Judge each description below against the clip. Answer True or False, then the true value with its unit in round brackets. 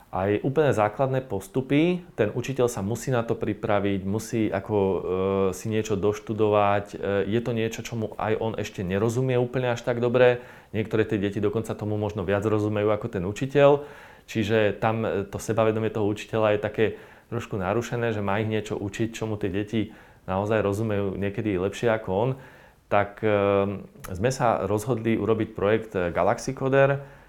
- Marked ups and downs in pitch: False (2.7 semitones)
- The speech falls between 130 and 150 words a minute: False (165 wpm)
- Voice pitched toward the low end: True (110 Hz)